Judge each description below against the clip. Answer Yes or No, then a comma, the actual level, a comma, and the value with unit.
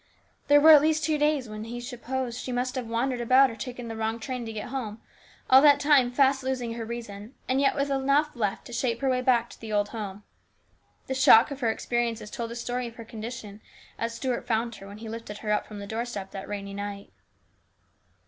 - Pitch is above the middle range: Yes, high, 235 Hz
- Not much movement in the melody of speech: No, average, 3.0 semitones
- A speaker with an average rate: No, fast, 225 wpm